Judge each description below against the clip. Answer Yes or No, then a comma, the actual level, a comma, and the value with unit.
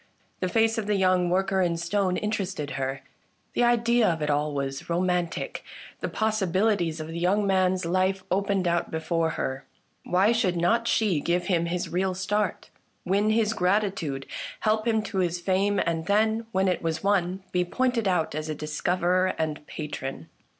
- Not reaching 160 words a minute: No, average, 175 wpm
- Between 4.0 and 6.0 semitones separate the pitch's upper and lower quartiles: No, average, 3.4 semitones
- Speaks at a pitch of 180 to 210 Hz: Yes, medium, 185 Hz